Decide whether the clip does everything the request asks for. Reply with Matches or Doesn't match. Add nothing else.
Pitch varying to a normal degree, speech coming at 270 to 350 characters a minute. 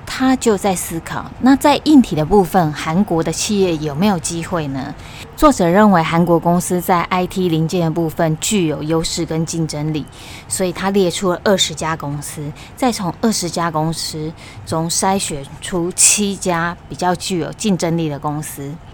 Doesn't match